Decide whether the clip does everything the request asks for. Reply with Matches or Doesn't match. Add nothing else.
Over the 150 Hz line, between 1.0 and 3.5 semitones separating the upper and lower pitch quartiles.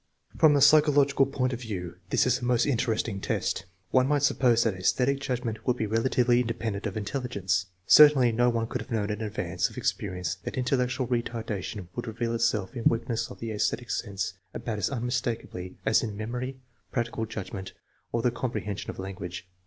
Doesn't match